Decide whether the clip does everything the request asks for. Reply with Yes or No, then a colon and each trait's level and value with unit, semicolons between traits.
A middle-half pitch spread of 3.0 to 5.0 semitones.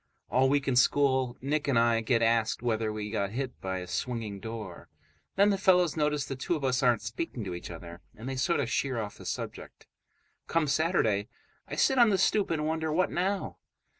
No: wide, 5.6 semitones